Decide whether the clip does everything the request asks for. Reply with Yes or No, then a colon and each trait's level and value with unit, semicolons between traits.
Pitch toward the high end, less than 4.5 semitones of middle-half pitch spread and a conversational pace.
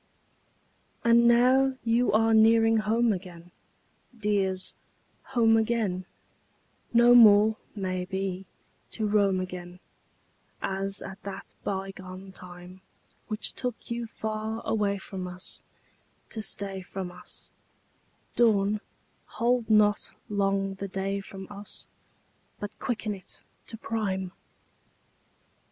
No: high, 205 Hz; average, 2.8 semitones; slow, 110 wpm